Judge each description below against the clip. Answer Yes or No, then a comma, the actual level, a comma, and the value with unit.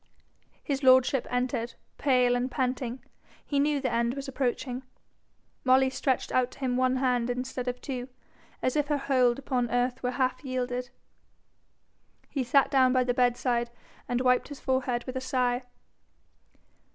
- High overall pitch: Yes, very high, 255 Hz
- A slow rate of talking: No, average, 155 wpm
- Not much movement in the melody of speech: Yes, narrow, 1.2 semitones